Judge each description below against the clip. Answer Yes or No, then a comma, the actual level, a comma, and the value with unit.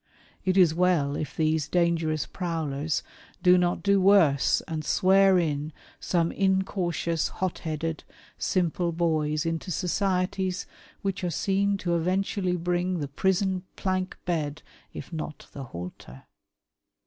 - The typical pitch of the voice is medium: Yes, medium, 175 Hz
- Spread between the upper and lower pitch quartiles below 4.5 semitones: Yes, average, 3.1 semitones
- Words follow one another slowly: Yes, slow, 125 wpm